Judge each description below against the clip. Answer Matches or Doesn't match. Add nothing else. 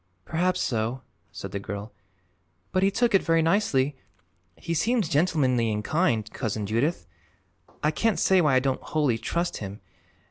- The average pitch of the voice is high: Doesn't match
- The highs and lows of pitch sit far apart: Matches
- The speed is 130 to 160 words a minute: Matches